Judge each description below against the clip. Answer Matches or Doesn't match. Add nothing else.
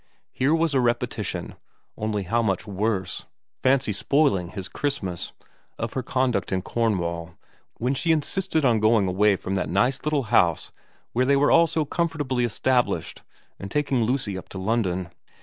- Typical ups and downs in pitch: Doesn't match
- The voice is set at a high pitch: Doesn't match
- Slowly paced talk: Doesn't match